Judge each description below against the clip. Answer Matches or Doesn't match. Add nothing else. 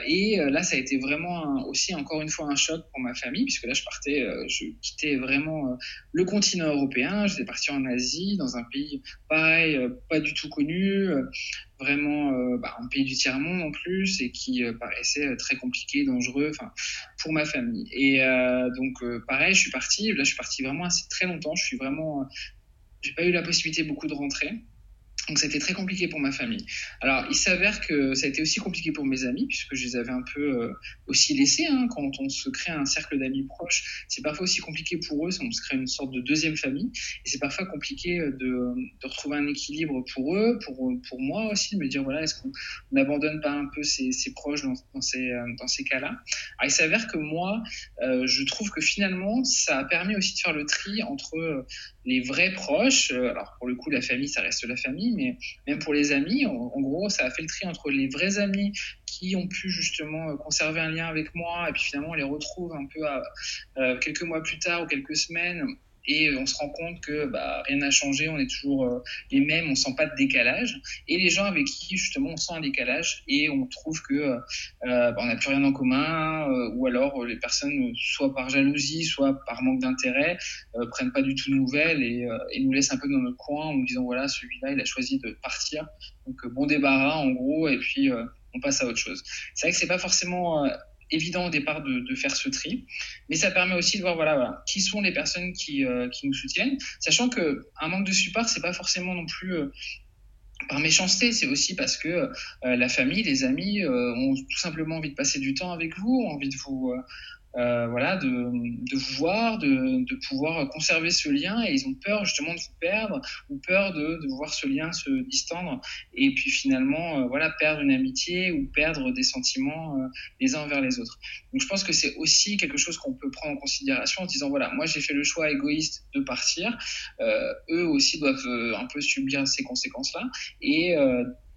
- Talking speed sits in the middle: Doesn't match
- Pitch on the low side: Doesn't match